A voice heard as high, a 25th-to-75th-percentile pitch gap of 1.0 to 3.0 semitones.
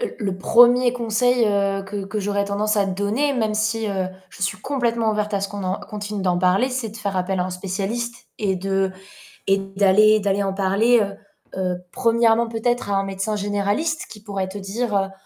Yes: high, 205 Hz; average, 2.7 semitones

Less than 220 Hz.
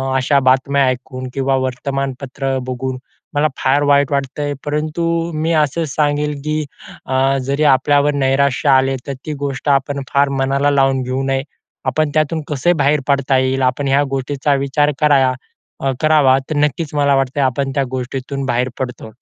Yes: medium, 140 Hz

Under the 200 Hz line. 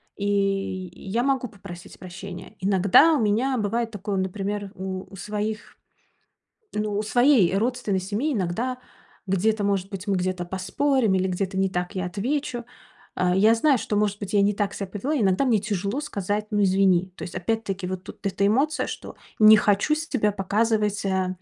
No: high, 205 Hz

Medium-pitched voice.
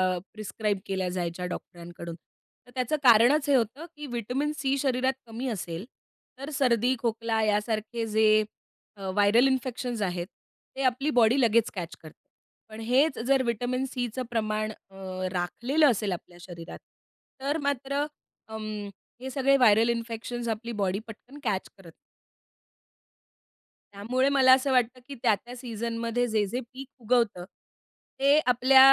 No: high, 235 Hz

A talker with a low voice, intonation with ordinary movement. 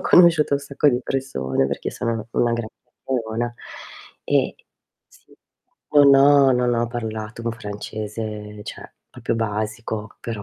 Yes: low, 115 Hz; average, 3.6 semitones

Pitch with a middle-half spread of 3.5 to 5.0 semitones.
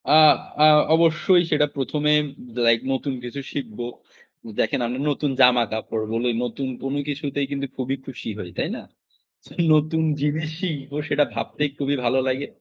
No: average, 3.0 semitones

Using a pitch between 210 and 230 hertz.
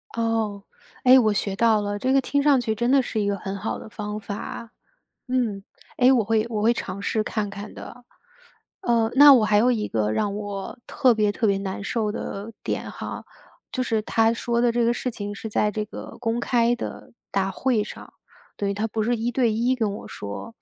Yes: high, 220 Hz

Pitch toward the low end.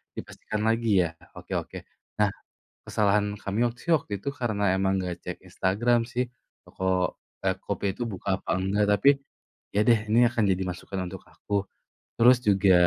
Yes: low, 105 Hz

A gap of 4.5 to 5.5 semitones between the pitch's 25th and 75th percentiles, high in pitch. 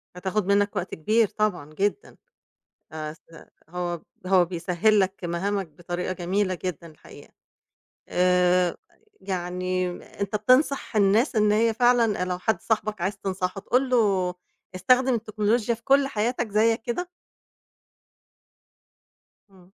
No: average, 3.6 semitones; high, 200 Hz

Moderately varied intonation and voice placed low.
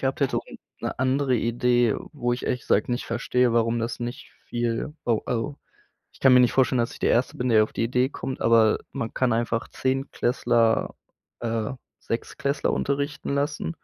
No: narrow, 2.3 semitones; low, 120 Hz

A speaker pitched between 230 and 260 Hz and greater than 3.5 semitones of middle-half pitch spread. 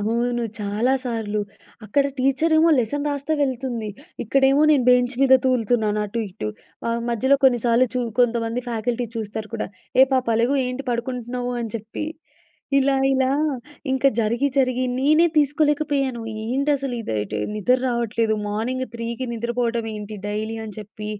No: high, 245 Hz; average, 2.9 semitones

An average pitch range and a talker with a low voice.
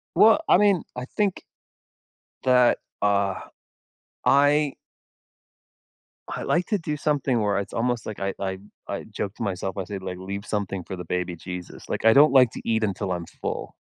No: wide, 6.7 semitones; low, 105 Hz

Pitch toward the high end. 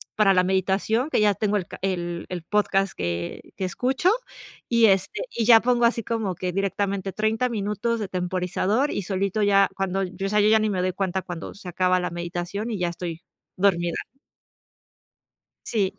Yes: high, 195 Hz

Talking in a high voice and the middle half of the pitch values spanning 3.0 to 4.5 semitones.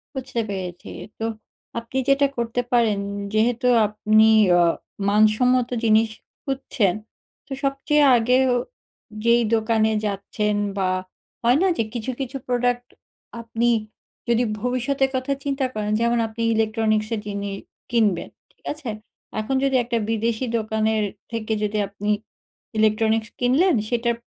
No: high, 230 Hz; narrow, 2.6 semitones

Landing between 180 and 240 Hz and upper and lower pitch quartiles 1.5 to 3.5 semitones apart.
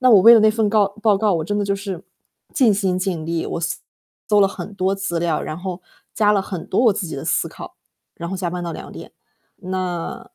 Yes: high, 195 Hz; average, 3.0 semitones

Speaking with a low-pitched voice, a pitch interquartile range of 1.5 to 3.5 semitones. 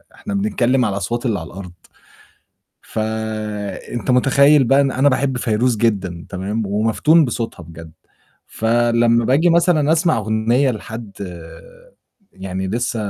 No: low, 115 Hz; average, 4.3 semitones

